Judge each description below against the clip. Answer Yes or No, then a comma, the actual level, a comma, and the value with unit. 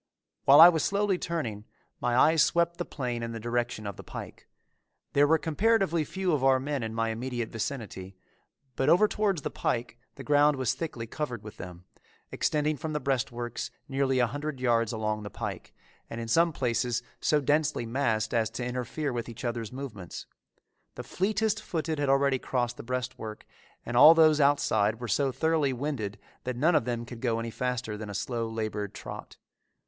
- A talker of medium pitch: No, low, 125 Hz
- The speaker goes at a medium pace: Yes, average, 185 wpm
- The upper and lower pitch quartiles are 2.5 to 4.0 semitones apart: No, average, 4.7 semitones